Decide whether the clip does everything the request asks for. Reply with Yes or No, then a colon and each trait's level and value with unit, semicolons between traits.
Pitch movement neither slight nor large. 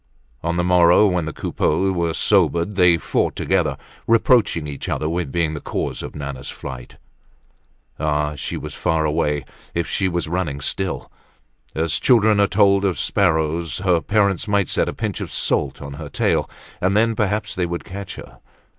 Yes: average, 4.1 semitones